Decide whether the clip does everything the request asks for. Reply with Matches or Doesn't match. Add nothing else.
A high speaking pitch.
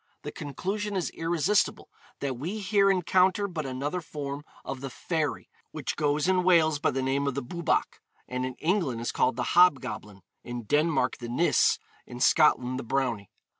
Doesn't match